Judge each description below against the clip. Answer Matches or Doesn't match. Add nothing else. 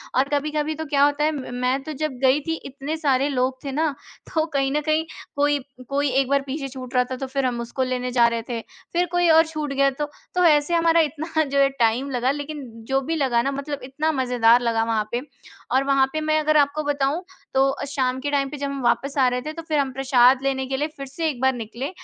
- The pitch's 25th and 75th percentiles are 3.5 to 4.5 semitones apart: Doesn't match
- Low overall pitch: Doesn't match